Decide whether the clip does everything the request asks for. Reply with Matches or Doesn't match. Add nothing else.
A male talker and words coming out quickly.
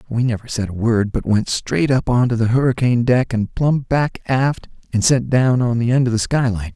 Matches